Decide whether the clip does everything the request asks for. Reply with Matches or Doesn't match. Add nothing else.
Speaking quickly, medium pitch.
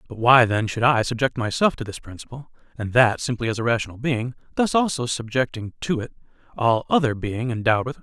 Doesn't match